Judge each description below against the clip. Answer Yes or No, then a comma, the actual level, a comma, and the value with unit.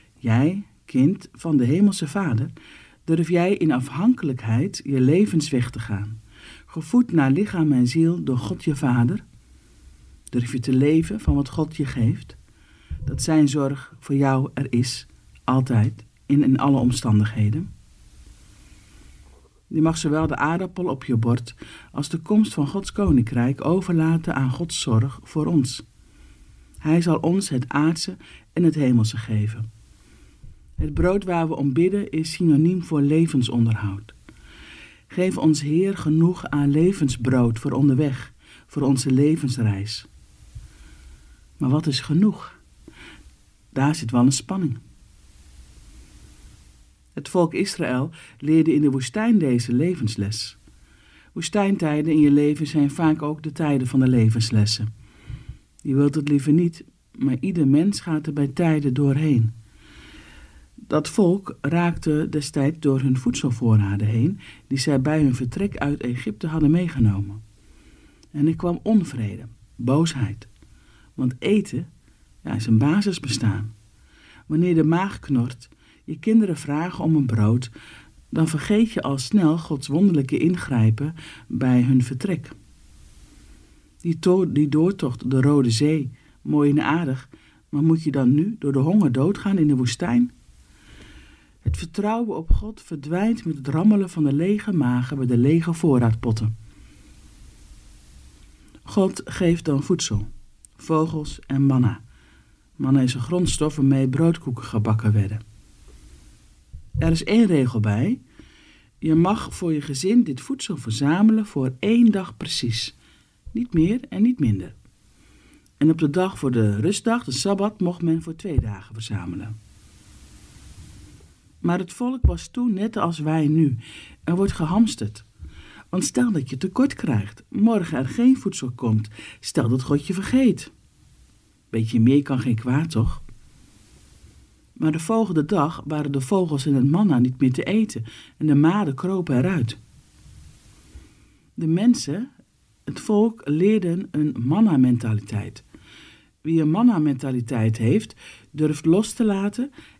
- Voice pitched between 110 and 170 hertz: Yes, medium, 140 Hz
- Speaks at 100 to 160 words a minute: Yes, average, 140 wpm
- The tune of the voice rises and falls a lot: Yes, wide, 6.5 semitones